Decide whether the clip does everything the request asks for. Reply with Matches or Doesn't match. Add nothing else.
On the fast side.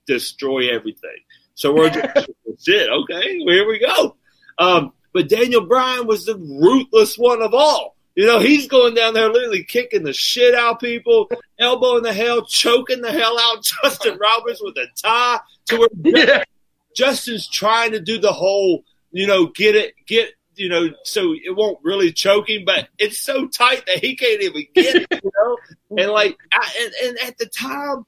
Doesn't match